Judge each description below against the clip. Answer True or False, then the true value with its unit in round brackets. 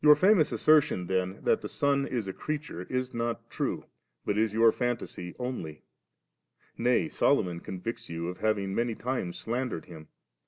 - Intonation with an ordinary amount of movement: False (5.7 semitones)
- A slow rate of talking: False (160 wpm)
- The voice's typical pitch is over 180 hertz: False (115 Hz)